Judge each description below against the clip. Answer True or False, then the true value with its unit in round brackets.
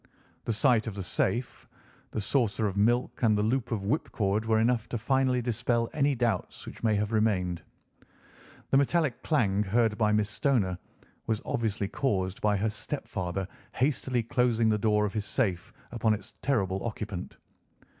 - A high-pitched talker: False (110 Hz)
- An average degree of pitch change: True (3.1 semitones)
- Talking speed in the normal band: True (165 wpm)